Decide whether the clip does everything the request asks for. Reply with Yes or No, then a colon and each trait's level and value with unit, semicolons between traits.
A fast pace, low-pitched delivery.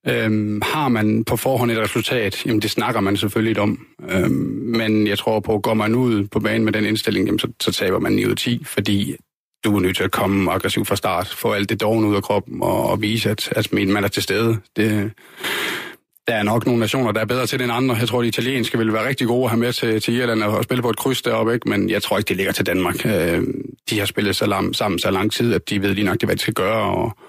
Yes: fast, 270 wpm; low, 110 Hz